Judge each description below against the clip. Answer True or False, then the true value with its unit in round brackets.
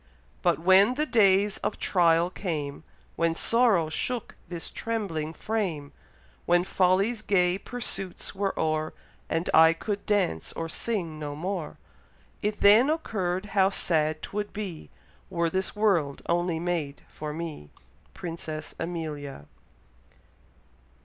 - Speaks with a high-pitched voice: False (175 Hz)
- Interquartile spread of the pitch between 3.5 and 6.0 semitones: True (4.1 semitones)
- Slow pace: True (125 wpm)